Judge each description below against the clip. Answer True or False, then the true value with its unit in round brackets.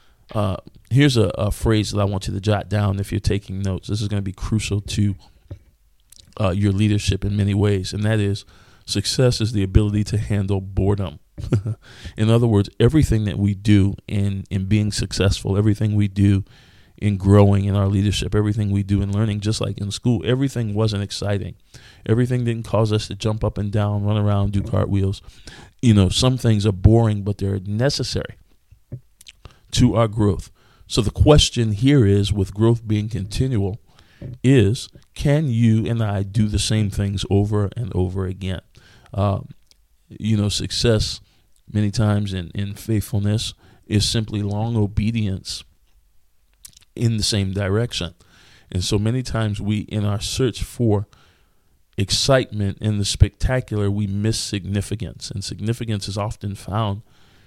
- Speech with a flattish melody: True (2.0 semitones)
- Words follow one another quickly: False (160 wpm)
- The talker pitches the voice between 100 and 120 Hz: True (105 Hz)